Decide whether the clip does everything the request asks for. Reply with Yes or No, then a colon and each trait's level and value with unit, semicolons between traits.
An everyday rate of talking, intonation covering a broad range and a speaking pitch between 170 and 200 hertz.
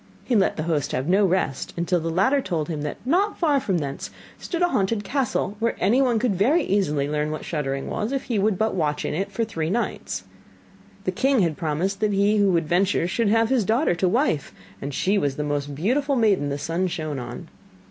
No: fast, 220 wpm; wide, 6.6 semitones; high, 190 Hz